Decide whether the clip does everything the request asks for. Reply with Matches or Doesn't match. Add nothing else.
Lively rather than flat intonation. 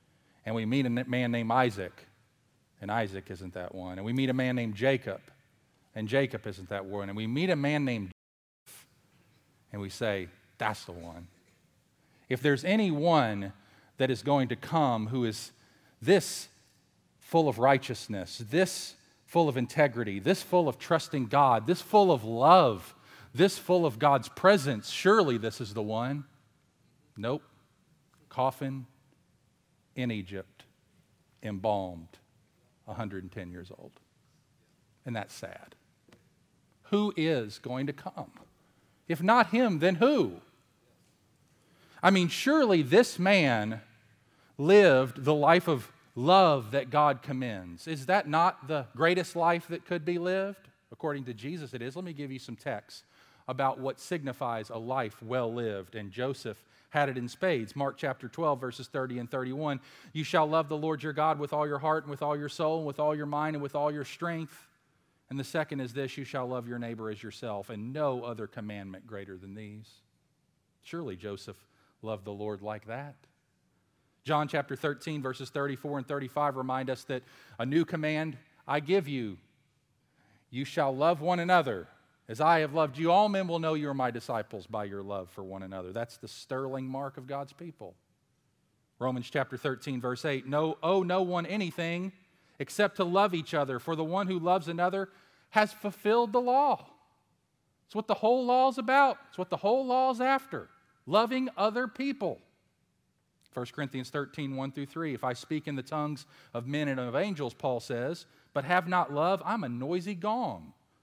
Matches